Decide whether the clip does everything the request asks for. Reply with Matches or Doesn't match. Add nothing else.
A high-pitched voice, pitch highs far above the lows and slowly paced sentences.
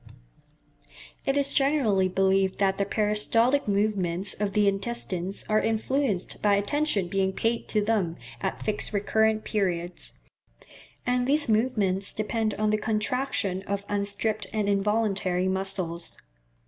Doesn't match